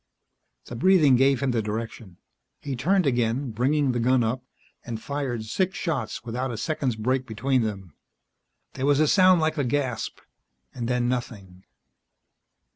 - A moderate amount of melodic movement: Yes, average, 3.7 semitones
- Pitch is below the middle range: Yes, low, 125 Hz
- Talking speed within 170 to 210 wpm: No, average, 155 wpm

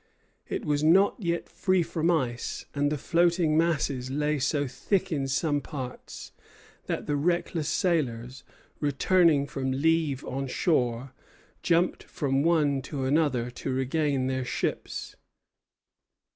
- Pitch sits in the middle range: Yes, medium, 145 Hz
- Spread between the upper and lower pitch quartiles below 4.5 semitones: Yes, average, 3.8 semitones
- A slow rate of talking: Yes, slow, 130 wpm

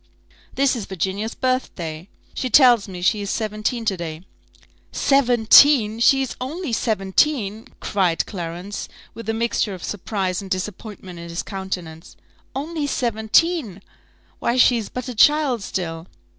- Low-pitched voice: No, high, 215 Hz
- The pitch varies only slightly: No, average, 5.1 semitones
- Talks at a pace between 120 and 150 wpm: Yes, average, 140 wpm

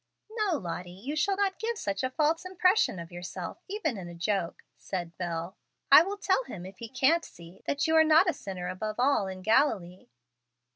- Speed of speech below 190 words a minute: No, average, 200 wpm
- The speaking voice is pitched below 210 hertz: No, high, 220 Hz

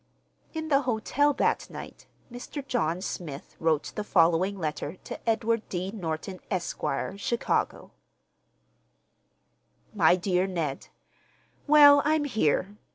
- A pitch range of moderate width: No, wide, 6.5 semitones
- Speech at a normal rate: No, slow, 105 wpm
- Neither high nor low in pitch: No, high, 200 Hz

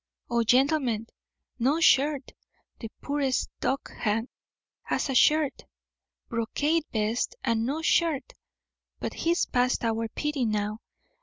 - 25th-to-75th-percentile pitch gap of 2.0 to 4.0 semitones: No, average, 4.5 semitones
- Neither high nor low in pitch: No, very high, 260 Hz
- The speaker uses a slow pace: Yes, slow, 110 wpm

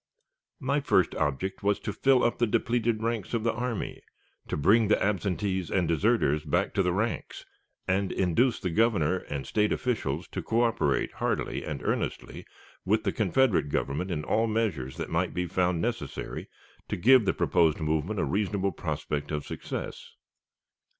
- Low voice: Yes, low, 100 Hz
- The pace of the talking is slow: No, average, 165 wpm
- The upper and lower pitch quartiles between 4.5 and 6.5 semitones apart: Yes, average, 5.2 semitones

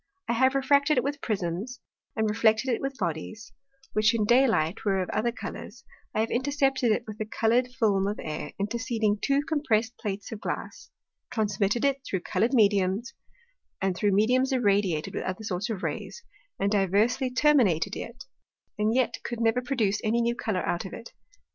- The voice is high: Yes, high, 220 Hz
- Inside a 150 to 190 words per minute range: Yes, average, 180 wpm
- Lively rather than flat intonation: No, average, 3.8 semitones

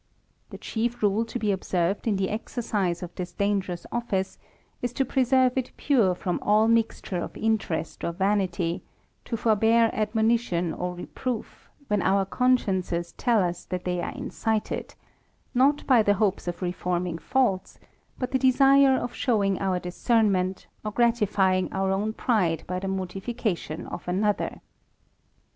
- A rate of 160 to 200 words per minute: No, average, 150 wpm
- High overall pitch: Yes, high, 205 Hz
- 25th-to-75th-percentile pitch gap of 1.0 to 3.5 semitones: No, average, 4.3 semitones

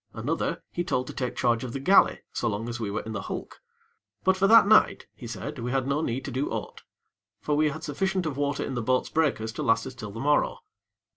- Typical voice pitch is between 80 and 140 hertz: Yes, low, 135 Hz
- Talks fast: Yes, fast, 245 wpm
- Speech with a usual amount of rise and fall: Yes, average, 4.7 semitones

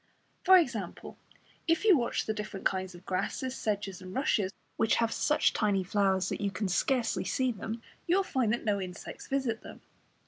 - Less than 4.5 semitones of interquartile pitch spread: No, average, 5.1 semitones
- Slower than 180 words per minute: No, average, 185 wpm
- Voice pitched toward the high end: Yes, high, 215 Hz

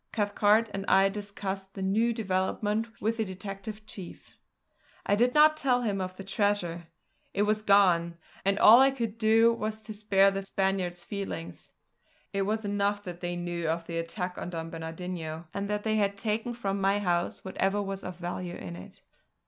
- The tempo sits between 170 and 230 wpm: Yes, average, 180 wpm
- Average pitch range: Yes, average, 3.0 semitones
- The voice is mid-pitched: No, high, 195 Hz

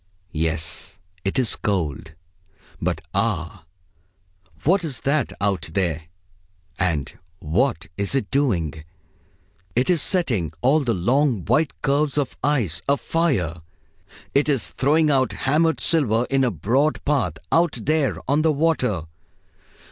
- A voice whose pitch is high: No, low, 130 Hz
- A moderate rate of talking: No, slow, 125 wpm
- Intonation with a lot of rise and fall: Yes, wide, 8.0 semitones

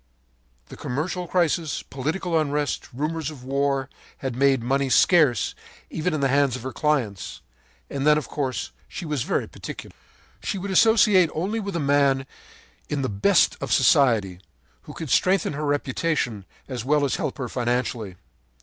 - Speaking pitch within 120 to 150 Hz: Yes, medium, 140 Hz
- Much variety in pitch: No, average, 3.6 semitones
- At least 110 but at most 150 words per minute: No, average, 160 wpm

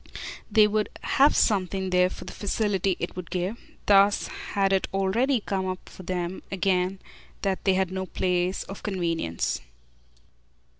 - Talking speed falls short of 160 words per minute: Yes, average, 150 wpm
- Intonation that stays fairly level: Yes, narrow, 1.6 semitones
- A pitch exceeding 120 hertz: Yes, high, 190 Hz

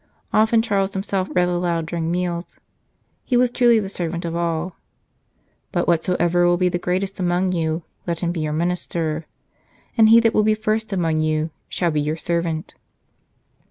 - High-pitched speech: No, medium, 175 Hz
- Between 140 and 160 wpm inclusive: No, average, 175 wpm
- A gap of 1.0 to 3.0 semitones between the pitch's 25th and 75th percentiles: Yes, average, 2.7 semitones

